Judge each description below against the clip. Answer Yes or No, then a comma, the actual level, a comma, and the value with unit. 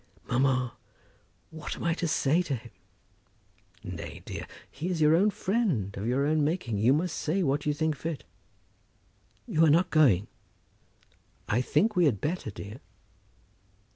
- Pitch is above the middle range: No, medium, 150 Hz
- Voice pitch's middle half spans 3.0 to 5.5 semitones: Yes, average, 5.0 semitones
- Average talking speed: Yes, average, 155 wpm